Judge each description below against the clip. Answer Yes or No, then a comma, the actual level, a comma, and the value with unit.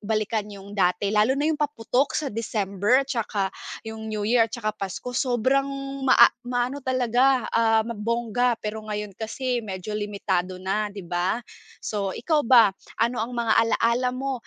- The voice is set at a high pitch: Yes, high, 225 Hz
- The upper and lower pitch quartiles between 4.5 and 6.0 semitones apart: No, average, 3.2 semitones